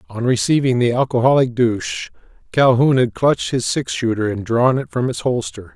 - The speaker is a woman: No, male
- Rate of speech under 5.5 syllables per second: Yes, 5.3 syllables/s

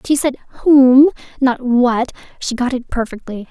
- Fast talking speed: No, average, 155 wpm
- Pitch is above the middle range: Yes, very high, 255 Hz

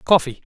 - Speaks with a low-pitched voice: No, medium, 155 Hz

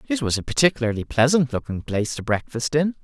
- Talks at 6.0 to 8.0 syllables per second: Yes, 6.4 syllables/s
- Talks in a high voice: No, low, 130 Hz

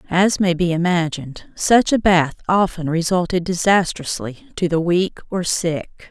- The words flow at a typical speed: Yes, average, 150 wpm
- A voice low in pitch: No, medium, 175 Hz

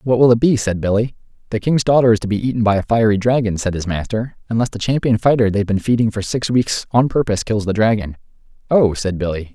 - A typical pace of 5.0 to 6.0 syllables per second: No, 6.3 syllables/s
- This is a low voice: Yes, low, 110 Hz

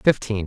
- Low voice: Yes, low, 110 Hz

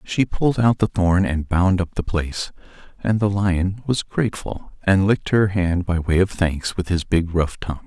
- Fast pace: Yes, fast, 215 wpm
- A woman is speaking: No, male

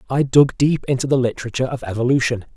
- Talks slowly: No, average, 190 wpm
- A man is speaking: Yes, male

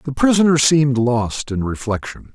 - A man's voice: Yes, male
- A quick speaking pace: No, average, 155 wpm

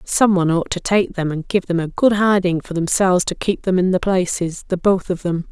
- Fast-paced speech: Yes, fast, 250 wpm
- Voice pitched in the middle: Yes, medium, 180 Hz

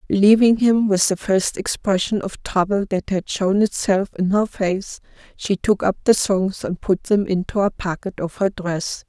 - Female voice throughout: Yes, female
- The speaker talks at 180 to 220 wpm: Yes, average, 190 wpm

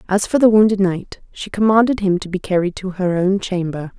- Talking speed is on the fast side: Yes, fast, 225 wpm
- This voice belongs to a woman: Yes, female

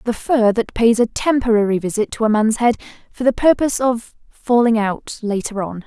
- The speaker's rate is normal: Yes, average, 195 wpm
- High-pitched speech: Yes, high, 230 Hz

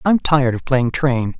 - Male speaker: Yes, male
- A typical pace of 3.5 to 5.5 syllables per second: Yes, 4.7 syllables/s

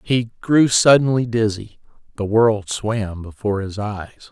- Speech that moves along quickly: No, average, 140 wpm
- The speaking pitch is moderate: No, low, 110 Hz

